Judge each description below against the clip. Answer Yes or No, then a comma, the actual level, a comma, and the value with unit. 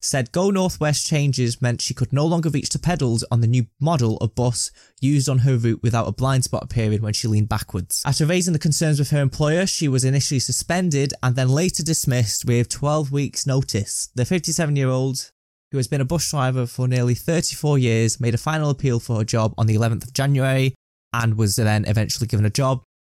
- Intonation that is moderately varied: Yes, average, 4.0 semitones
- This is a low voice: Yes, low, 130 Hz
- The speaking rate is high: Yes, fast, 215 wpm